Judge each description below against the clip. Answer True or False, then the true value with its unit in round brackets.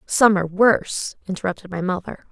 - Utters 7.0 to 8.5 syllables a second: False (6.0 syllables/s)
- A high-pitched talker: True (195 Hz)